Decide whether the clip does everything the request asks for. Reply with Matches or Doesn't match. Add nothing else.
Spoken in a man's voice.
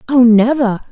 Doesn't match